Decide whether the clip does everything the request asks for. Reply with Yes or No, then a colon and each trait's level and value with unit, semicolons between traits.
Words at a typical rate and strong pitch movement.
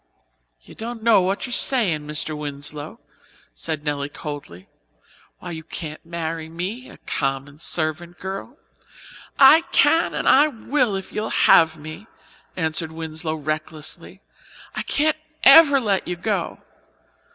No: slow, 130 wpm; wide, 6.3 semitones